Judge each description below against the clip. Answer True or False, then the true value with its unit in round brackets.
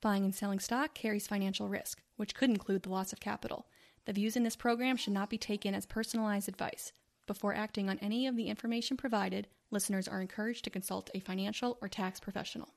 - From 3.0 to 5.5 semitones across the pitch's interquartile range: False (2.5 semitones)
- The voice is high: True (210 Hz)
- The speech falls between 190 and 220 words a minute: True (205 wpm)